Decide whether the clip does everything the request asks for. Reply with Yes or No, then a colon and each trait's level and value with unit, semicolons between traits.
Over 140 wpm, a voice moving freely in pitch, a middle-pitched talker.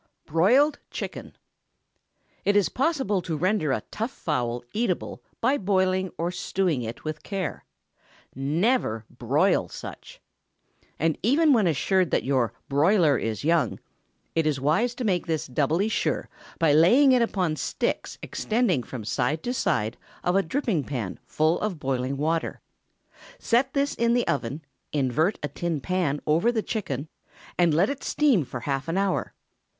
Yes: average, 155 wpm; wide, 6.8 semitones; medium, 170 Hz